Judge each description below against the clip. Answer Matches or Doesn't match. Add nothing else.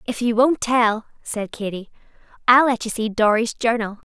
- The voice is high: Matches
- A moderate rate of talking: Matches